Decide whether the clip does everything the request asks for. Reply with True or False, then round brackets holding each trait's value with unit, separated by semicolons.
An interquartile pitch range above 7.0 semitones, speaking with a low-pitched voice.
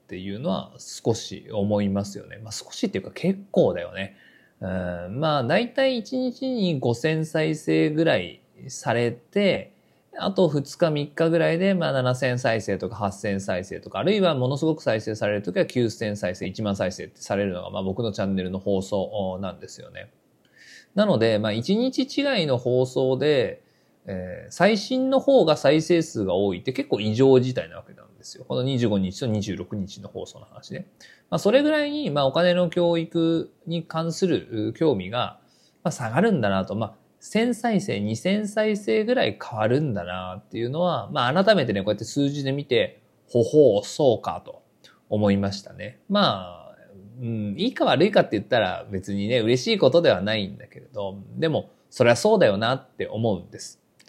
True (8.8 semitones; 125 Hz)